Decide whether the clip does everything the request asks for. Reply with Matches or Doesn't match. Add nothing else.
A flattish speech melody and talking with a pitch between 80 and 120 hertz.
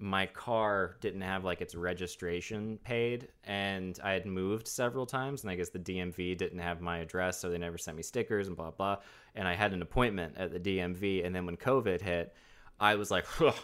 Matches